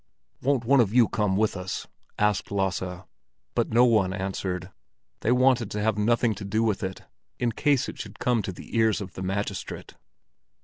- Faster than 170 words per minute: Yes, average, 185 wpm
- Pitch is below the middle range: Yes, low, 105 Hz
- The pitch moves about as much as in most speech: Yes, average, 3.5 semitones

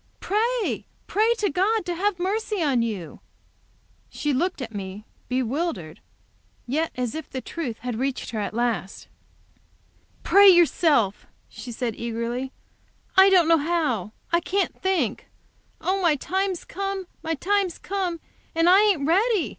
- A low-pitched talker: No, very high, 330 Hz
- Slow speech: No, average, 145 wpm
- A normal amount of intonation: No, wide, 7.8 semitones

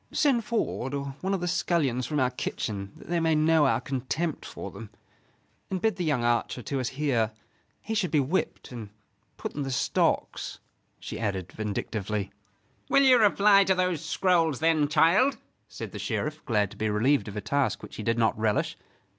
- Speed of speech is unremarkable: Yes, average, 190 wpm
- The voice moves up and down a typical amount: No, wide, 7.3 semitones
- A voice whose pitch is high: No, medium, 145 Hz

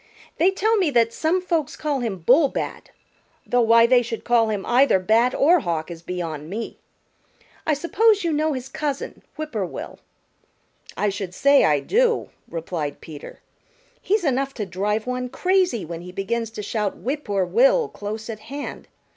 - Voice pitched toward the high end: Yes, high, 240 Hz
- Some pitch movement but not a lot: No, wide, 7.4 semitones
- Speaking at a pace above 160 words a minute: Yes, average, 170 wpm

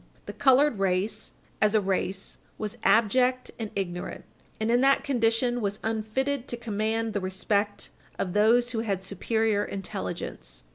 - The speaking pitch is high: Yes, high, 220 Hz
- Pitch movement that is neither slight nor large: Yes, average, 3.2 semitones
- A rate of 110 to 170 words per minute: Yes, average, 145 wpm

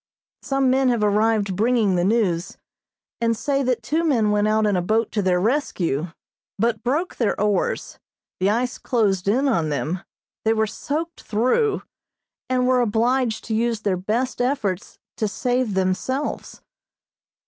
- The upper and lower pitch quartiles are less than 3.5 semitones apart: No, average, 4.0 semitones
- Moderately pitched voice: No, high, 225 Hz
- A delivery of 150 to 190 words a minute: Yes, average, 155 wpm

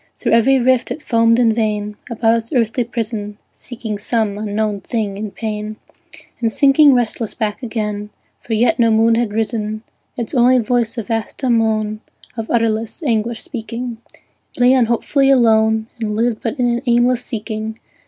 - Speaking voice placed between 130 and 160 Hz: No, high, 230 Hz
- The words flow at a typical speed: Yes, average, 165 wpm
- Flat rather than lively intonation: Yes, narrow, 1.9 semitones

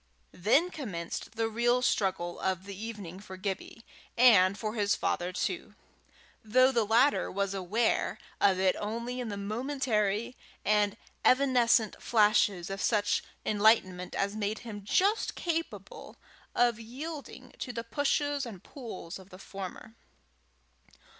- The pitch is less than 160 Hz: No, high, 215 Hz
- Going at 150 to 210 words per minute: No, slow, 135 wpm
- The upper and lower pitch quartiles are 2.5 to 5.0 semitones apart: Yes, average, 3.8 semitones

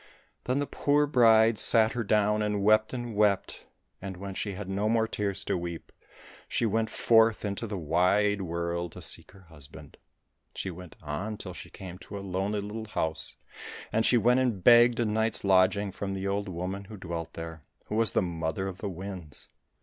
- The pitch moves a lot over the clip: No, average, 3.2 semitones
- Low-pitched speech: Yes, low, 100 Hz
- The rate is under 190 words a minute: No, average, 195 wpm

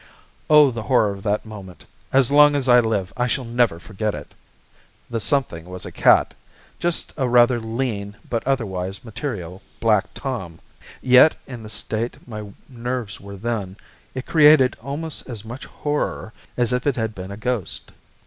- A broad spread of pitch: No, average, 4.0 semitones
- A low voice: Yes, low, 115 Hz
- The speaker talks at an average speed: Yes, average, 170 wpm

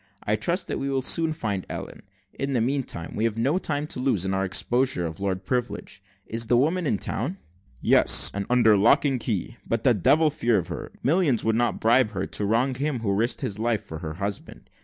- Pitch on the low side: Yes, low, 115 Hz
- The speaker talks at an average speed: No, fast, 220 wpm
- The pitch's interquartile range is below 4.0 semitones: No, average, 5.0 semitones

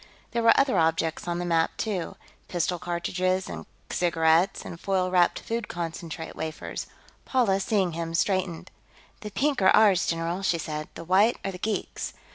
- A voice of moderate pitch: Yes, medium, 180 Hz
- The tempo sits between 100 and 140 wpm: No, average, 165 wpm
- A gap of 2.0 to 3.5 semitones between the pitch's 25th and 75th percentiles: Yes, average, 2.8 semitones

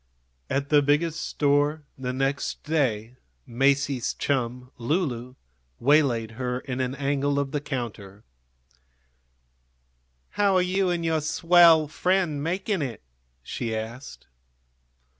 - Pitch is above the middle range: No, medium, 140 Hz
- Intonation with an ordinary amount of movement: Yes, average, 3.9 semitones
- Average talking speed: No, slow, 115 wpm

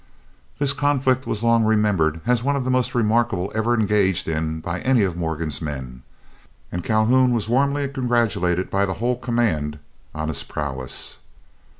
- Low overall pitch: Yes, low, 110 Hz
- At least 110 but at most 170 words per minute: Yes, average, 160 wpm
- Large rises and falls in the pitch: Yes, wide, 7.1 semitones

